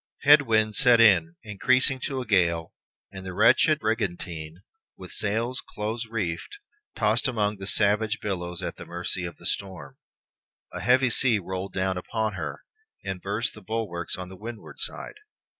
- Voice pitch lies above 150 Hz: No, low, 105 Hz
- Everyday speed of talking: Yes, average, 160 wpm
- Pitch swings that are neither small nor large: Yes, average, 3.8 semitones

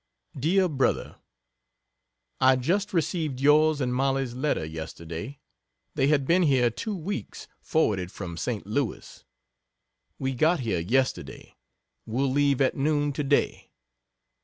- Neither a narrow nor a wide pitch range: Yes, average, 4.0 semitones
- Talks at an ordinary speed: No, slow, 125 wpm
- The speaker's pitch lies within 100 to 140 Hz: Yes, low, 135 Hz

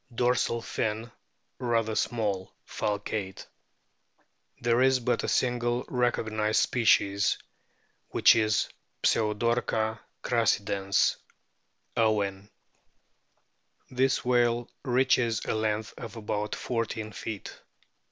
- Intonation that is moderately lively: No, narrow, 2.2 semitones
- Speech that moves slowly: Yes, slow, 90 wpm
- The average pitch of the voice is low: Yes, low, 115 Hz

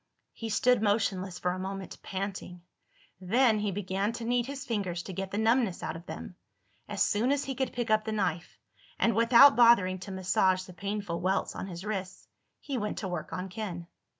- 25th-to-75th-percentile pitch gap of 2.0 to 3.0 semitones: No, average, 3.6 semitones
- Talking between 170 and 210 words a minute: Yes, average, 190 wpm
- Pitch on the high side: Yes, high, 200 Hz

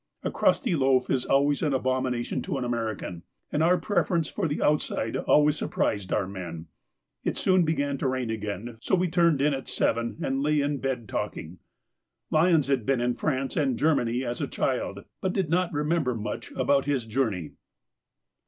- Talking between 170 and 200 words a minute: Yes, average, 180 wpm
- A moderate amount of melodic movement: Yes, average, 4.3 semitones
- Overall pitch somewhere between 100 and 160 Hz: Yes, low, 135 Hz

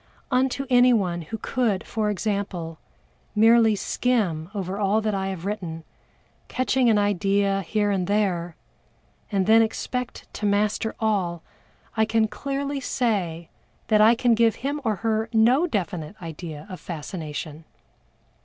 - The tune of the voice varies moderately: Yes, average, 3.8 semitones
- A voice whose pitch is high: Yes, high, 210 Hz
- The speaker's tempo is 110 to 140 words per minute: Yes, slow, 135 wpm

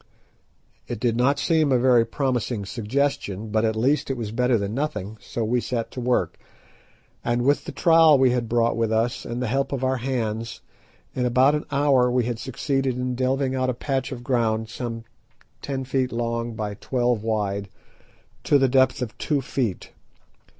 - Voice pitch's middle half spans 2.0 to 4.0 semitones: Yes, narrow, 2.6 semitones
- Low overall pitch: Yes, low, 125 Hz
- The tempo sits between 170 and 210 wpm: Yes, average, 180 wpm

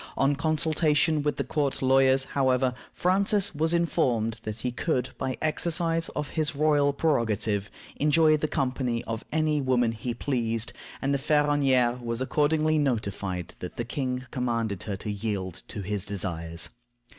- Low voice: Yes, low, 130 Hz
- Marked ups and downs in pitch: No, average, 4.9 semitones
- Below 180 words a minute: Yes, average, 155 wpm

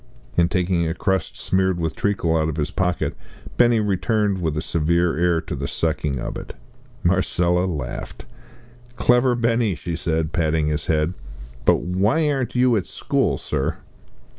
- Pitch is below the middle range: Yes, very low, 90 Hz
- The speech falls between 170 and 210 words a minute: No, average, 160 wpm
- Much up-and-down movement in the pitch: No, average, 4.2 semitones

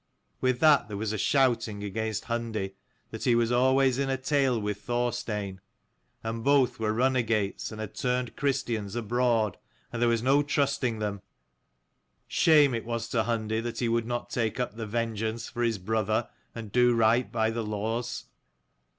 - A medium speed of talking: Yes, average, 175 wpm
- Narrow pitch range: Yes, narrow, 2.2 semitones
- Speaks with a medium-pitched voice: No, low, 115 Hz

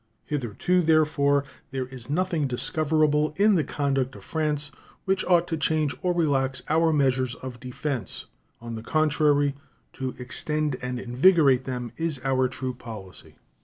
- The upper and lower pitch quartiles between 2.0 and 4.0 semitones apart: Yes, average, 3.5 semitones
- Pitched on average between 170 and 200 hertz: No, medium, 145 Hz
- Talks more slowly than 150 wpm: Yes, average, 140 wpm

